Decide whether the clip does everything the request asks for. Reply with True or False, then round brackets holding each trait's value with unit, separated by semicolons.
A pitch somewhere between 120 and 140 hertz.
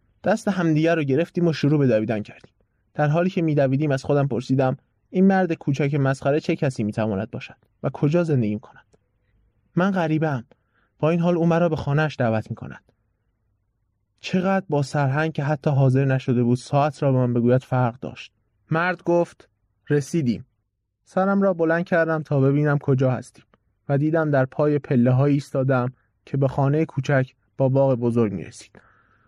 True (135 Hz)